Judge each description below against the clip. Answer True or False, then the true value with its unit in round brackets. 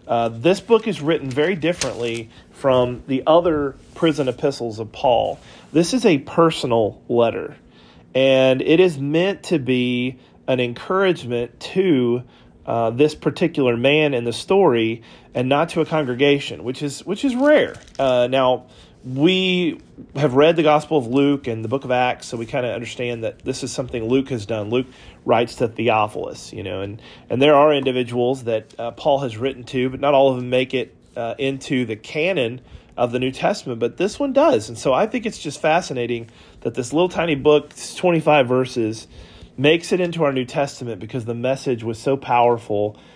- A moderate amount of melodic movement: True (4.3 semitones)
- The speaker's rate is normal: True (190 wpm)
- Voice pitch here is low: True (130 Hz)